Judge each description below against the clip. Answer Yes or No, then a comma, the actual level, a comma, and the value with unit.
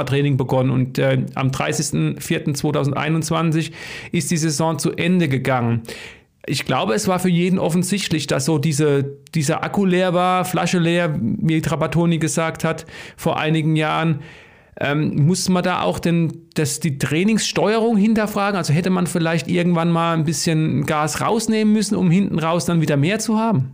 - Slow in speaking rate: No, average, 160 wpm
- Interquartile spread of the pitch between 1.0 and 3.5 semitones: Yes, average, 2.7 semitones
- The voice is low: No, medium, 165 Hz